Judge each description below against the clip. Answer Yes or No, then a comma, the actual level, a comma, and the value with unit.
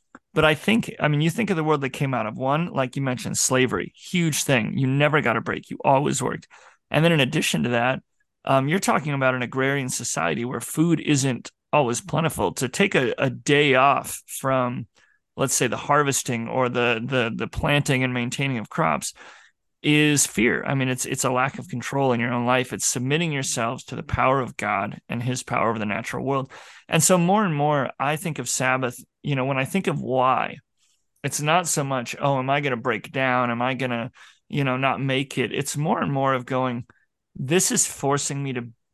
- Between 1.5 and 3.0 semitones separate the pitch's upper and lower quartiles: Yes, average, 2.7 semitones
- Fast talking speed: Yes, fast, 220 wpm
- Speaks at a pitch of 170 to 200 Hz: No, low, 135 Hz